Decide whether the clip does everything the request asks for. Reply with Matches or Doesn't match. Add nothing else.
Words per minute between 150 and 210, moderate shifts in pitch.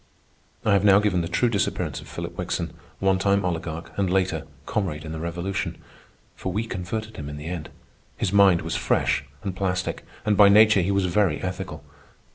Matches